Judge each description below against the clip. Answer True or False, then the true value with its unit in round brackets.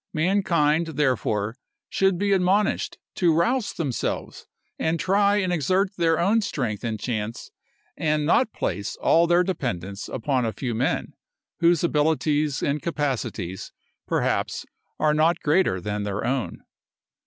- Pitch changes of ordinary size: False (6.6 semitones)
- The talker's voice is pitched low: False (155 Hz)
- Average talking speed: False (130 wpm)